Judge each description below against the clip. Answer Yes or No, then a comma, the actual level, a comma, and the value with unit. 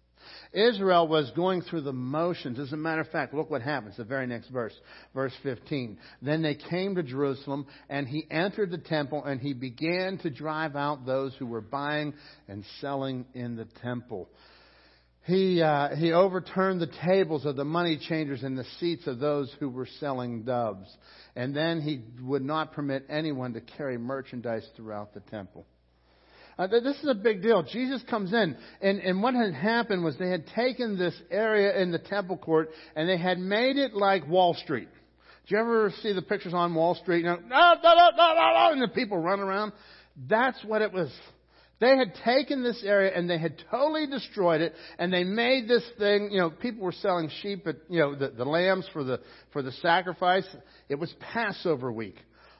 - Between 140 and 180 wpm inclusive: No, average, 190 wpm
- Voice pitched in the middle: Yes, medium, 165 Hz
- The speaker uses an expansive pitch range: Yes, wide, 5.9 semitones